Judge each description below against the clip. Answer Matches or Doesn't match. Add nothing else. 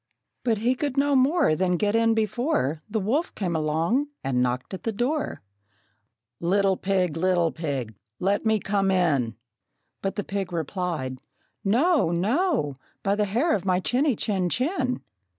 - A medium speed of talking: Matches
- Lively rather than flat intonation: Matches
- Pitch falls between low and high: Doesn't match